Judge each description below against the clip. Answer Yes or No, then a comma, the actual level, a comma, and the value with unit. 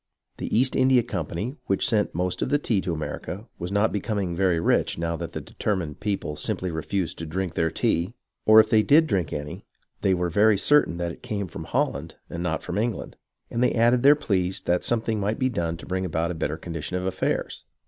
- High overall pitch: No, very low, 95 Hz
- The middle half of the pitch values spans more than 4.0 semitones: Yes, average, 4.5 semitones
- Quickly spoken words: Yes, fast, 220 wpm